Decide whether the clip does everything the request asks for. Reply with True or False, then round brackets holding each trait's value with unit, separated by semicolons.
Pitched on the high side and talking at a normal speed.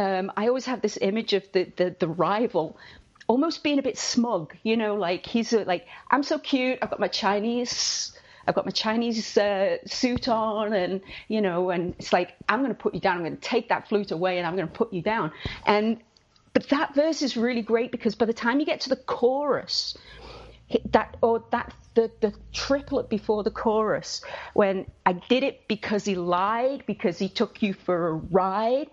False (220 Hz; 210 wpm)